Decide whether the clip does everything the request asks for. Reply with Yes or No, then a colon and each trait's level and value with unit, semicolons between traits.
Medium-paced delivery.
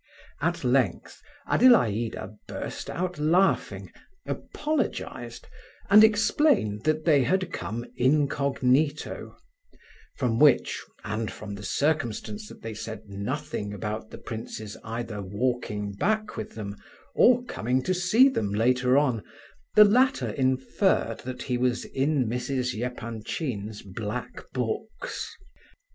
No: slow, 115 wpm